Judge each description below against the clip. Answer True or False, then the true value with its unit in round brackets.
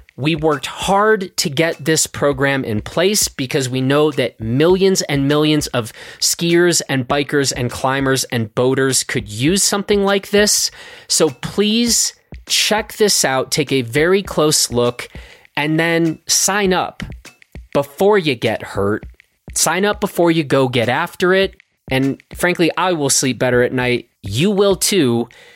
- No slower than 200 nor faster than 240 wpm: False (155 wpm)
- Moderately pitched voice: True (150 Hz)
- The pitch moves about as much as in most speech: False (6.4 semitones)